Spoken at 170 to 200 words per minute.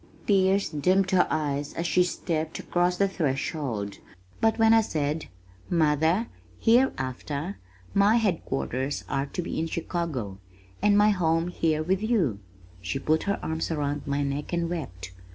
No: average, 150 wpm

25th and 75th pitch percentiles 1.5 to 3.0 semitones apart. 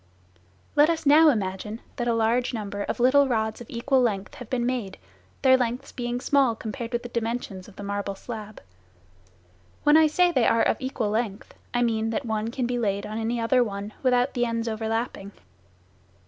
Yes: narrow, 2.6 semitones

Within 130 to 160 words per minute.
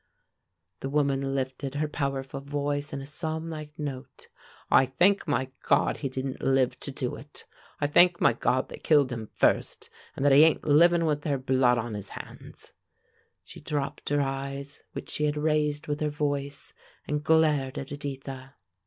No: average, 170 wpm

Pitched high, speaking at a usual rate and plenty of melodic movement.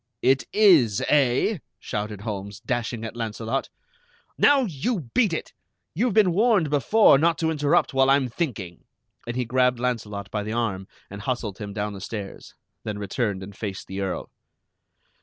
No: low, 120 Hz; average, 160 wpm; wide, 6.5 semitones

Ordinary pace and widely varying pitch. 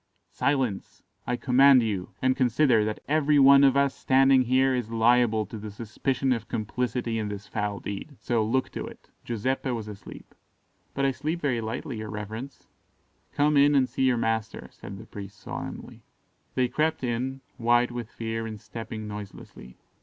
No: average, 170 wpm; average, 3.5 semitones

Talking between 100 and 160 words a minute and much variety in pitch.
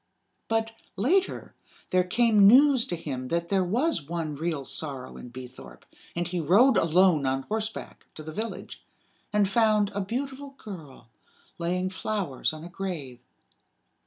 Yes: average, 145 wpm; wide, 6.0 semitones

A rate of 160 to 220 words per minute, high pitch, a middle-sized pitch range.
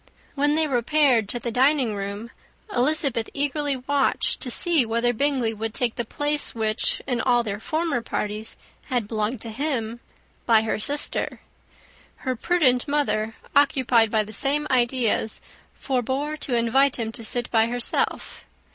No: average, 150 wpm; high, 245 Hz; average, 4.0 semitones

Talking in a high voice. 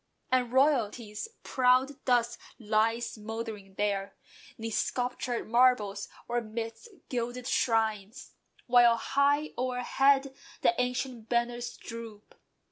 Yes: high, 240 Hz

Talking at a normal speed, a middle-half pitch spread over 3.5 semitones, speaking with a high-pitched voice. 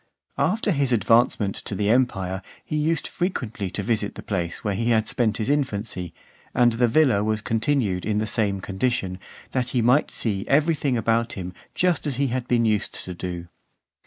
No: average, 190 wpm; average, 4.3 semitones; low, 115 Hz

